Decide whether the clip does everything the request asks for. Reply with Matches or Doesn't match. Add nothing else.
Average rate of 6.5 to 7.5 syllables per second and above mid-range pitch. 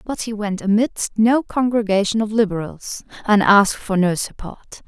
Doesn't match